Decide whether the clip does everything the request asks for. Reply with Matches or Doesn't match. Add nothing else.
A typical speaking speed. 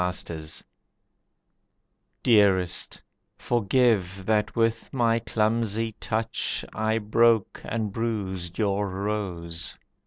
Doesn't match